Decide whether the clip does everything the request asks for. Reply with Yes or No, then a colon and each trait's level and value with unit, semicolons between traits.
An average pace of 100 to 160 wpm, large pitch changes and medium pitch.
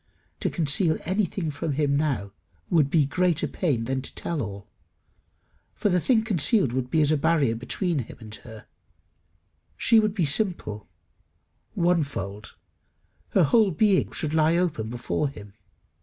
Yes: average, 155 wpm; wide, 6.0 semitones; medium, 155 Hz